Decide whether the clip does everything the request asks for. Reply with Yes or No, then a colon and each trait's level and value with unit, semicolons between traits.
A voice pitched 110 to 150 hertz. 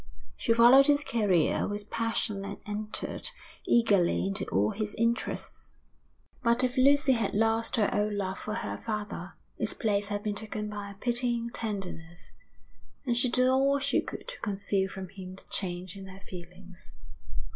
No: high, 210 Hz